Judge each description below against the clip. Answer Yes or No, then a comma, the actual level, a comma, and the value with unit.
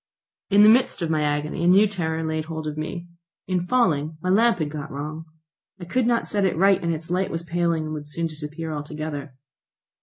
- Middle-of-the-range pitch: Yes, medium, 165 Hz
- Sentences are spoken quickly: Yes, fast, 215 wpm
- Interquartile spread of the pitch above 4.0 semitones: No, average, 3.1 semitones